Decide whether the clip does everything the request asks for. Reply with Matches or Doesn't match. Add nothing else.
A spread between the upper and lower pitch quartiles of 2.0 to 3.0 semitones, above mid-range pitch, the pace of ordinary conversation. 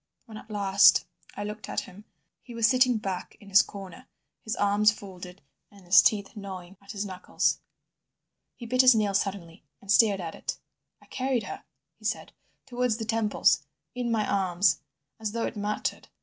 Matches